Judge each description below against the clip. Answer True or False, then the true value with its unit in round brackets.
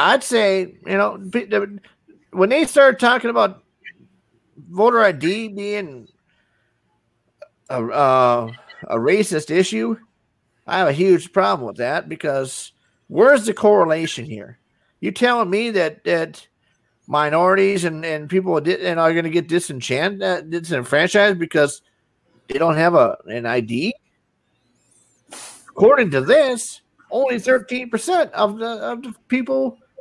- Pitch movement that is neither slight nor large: False (6.5 semitones)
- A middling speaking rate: False (130 wpm)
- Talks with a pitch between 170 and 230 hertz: True (190 Hz)